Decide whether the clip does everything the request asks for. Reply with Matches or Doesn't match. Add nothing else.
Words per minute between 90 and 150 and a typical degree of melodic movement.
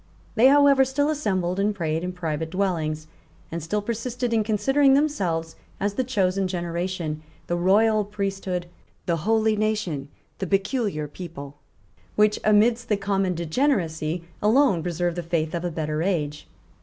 Matches